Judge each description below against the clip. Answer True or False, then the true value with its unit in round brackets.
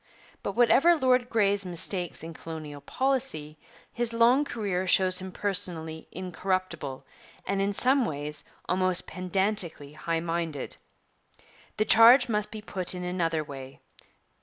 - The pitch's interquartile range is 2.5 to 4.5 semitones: False (5.0 semitones)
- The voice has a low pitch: False (185 Hz)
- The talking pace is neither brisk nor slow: False (130 wpm)